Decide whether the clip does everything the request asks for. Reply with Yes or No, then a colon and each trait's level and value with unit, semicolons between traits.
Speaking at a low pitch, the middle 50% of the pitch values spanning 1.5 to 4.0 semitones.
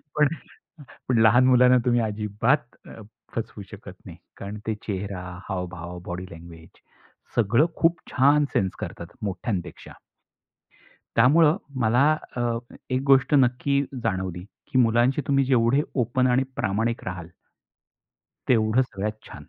No: low, 115 Hz; average, 5.0 semitones